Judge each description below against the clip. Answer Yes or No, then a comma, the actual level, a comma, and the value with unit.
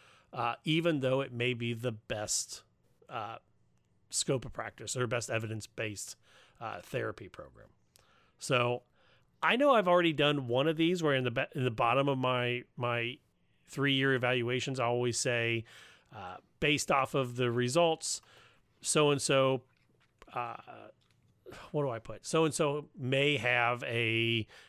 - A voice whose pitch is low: Yes, low, 125 Hz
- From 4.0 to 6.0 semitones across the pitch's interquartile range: No, average, 3.3 semitones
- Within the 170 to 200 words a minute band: No, average, 150 wpm